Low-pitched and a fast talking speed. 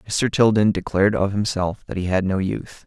Yes: low, 100 Hz; fast, 210 wpm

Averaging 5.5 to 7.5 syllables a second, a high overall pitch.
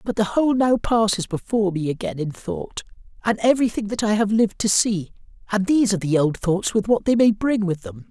Yes: 5.8 syllables/s; high, 205 Hz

